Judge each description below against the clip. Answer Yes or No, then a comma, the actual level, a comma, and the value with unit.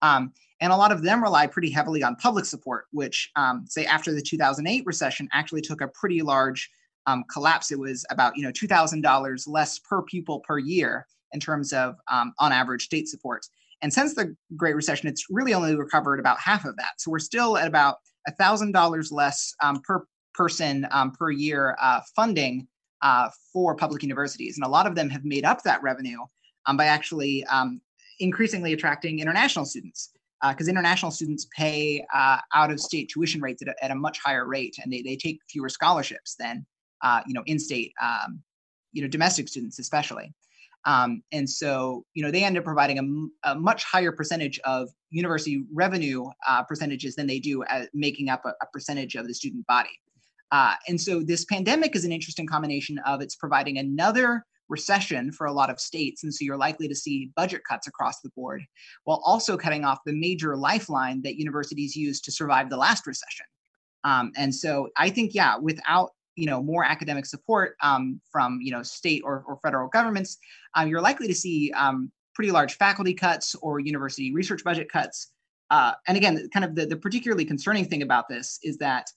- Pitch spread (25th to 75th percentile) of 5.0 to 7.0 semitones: No, average, 4.0 semitones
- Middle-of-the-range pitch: Yes, medium, 150 Hz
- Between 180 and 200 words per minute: Yes, average, 195 wpm